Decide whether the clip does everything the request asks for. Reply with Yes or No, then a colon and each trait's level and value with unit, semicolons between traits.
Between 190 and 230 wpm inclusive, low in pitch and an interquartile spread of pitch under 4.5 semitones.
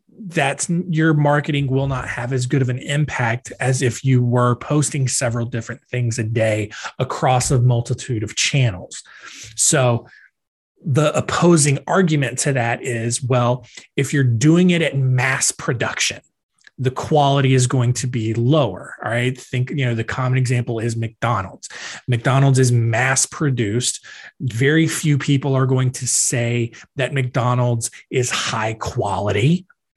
No: average, 150 wpm; low, 125 Hz; average, 2.9 semitones